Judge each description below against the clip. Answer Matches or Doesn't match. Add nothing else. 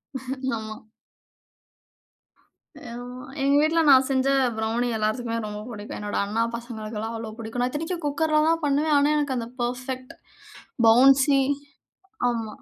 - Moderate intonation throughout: Matches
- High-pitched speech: Matches